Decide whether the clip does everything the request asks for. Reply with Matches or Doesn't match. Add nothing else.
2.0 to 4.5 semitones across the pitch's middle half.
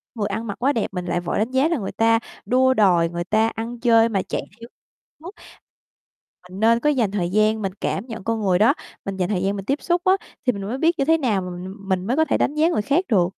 Doesn't match